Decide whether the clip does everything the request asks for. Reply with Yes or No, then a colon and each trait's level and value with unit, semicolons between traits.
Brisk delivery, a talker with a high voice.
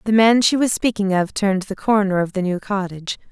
Yes: fast, 235 wpm; high, 200 Hz